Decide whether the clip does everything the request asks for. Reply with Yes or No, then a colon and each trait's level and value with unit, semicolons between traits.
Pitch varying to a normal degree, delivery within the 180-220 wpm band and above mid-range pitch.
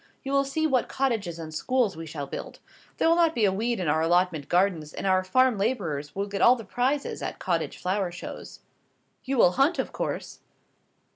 No: wide, 6.9 semitones; fast, 205 wpm; high, 200 Hz